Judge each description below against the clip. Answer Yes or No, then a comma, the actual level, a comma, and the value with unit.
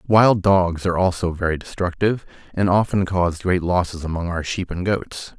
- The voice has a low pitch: Yes, very low, 90 Hz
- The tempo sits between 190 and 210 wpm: No, average, 180 wpm